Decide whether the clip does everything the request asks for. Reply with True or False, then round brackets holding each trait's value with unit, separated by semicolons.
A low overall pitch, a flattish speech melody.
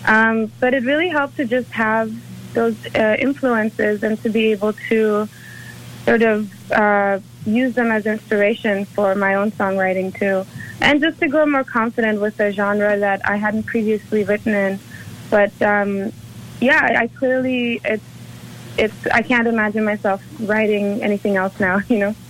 False (215 Hz; 2.2 semitones)